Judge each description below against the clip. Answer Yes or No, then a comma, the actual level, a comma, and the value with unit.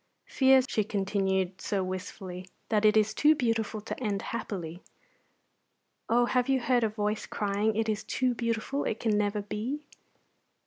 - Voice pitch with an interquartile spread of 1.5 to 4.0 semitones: Yes, average, 2.9 semitones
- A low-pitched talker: No, high, 215 Hz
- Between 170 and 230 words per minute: No, average, 160 wpm